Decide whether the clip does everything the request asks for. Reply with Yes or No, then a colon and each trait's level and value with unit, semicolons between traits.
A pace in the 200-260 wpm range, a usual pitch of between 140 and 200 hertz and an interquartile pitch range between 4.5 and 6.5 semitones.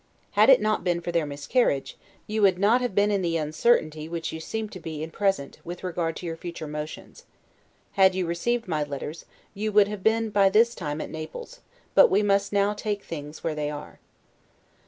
Yes: fast, 205 wpm; medium, 185 Hz; average, 4.8 semitones